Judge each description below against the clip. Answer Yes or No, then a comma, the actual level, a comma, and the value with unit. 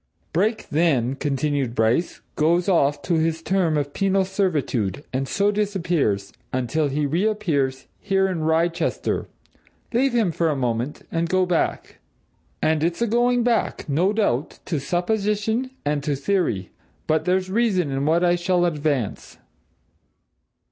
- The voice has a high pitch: No, medium, 165 Hz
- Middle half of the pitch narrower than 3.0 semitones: No, average, 5.2 semitones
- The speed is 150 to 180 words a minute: No, average, 140 wpm